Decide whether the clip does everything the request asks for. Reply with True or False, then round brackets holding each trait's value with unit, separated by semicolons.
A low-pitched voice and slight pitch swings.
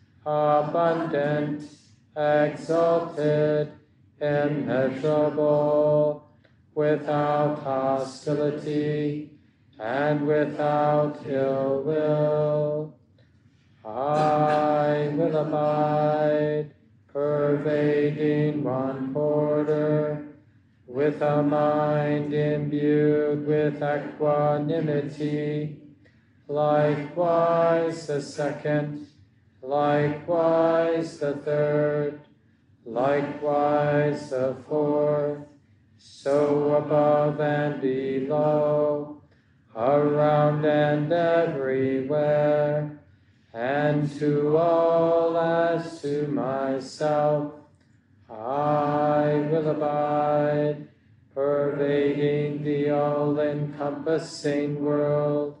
False (150 Hz; 0.7 semitones)